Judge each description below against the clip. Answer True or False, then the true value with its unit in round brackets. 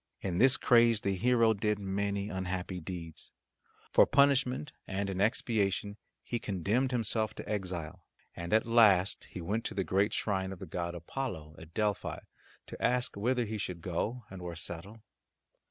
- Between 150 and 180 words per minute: True (165 wpm)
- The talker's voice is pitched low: True (100 Hz)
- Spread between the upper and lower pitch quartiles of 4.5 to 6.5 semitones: False (4.0 semitones)